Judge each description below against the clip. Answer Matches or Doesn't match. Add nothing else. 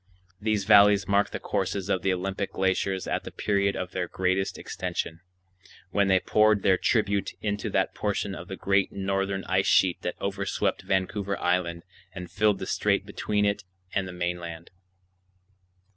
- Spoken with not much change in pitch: Matches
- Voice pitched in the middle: Doesn't match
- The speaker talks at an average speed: Matches